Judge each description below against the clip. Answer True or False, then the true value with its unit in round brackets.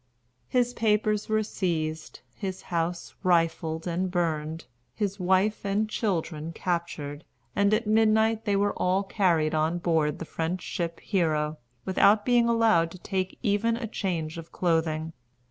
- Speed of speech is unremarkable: True (145 wpm)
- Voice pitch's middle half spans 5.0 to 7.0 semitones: False (4.4 semitones)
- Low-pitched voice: False (185 Hz)